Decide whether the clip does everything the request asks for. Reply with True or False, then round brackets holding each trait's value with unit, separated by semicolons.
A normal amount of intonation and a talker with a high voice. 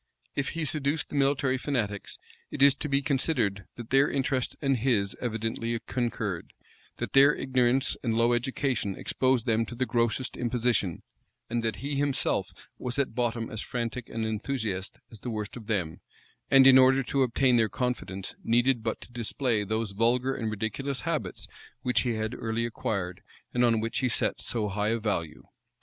False (3.2 semitones; 120 Hz)